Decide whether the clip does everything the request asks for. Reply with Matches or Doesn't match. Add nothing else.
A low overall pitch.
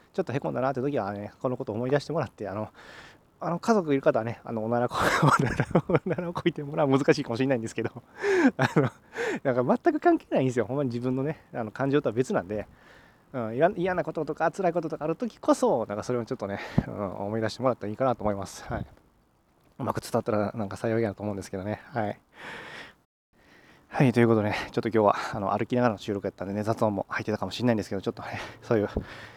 Matches